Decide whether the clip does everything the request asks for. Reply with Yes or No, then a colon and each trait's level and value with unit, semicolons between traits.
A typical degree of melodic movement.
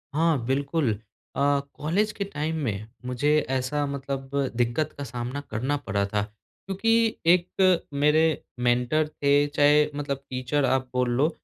Yes: average, 3.6 semitones